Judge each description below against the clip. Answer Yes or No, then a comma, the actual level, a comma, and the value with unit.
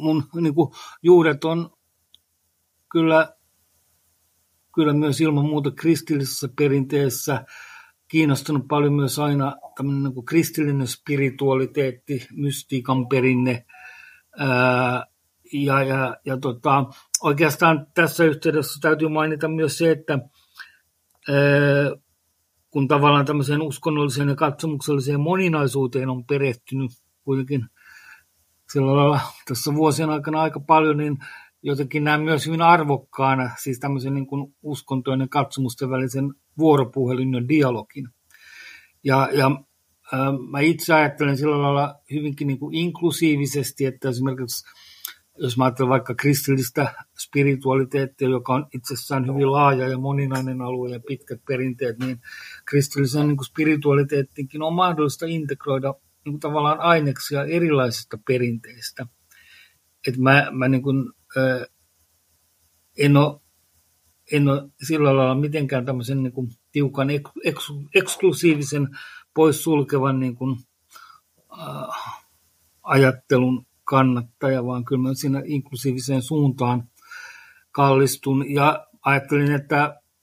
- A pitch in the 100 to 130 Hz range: No, medium, 140 Hz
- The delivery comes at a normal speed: Yes, average, 105 wpm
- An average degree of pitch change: No, narrow, 2.3 semitones